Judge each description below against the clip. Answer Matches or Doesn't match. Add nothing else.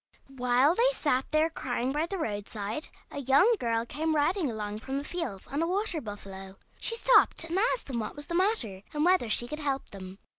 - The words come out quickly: Matches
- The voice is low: Doesn't match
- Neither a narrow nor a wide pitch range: Doesn't match